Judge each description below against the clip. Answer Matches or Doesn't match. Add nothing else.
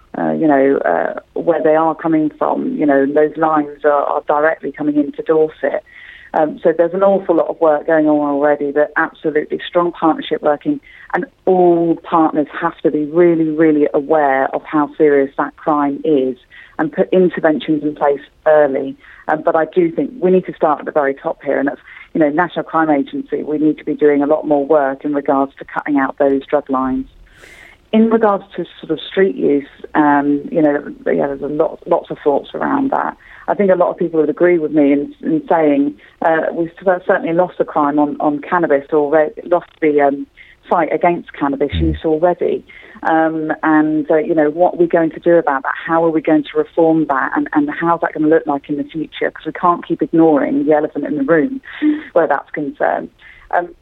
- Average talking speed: Doesn't match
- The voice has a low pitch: Doesn't match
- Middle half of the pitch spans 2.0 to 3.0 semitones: Matches